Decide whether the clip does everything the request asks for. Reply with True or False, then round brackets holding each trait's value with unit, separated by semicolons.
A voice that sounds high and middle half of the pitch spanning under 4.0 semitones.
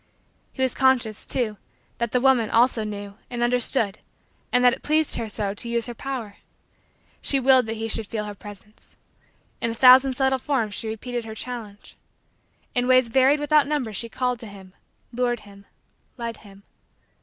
True (235 Hz; 3.1 semitones)